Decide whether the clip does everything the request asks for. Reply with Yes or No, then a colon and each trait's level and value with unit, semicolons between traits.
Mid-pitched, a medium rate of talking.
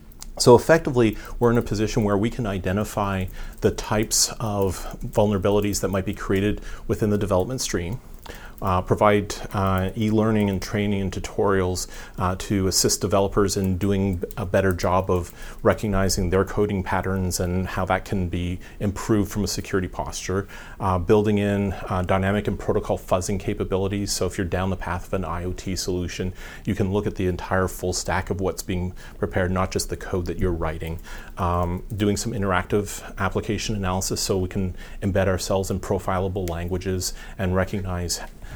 No: very low, 95 Hz; average, 170 wpm